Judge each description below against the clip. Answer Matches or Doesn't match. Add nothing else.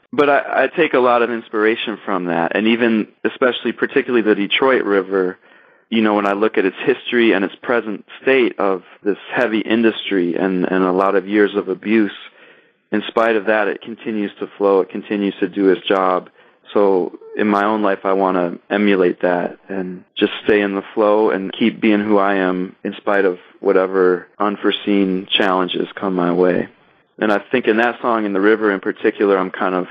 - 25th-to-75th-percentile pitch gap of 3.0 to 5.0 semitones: Doesn't match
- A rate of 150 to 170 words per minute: Doesn't match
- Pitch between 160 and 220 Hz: Doesn't match